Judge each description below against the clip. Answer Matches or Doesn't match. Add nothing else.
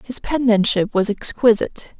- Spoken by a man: Doesn't match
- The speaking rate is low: Matches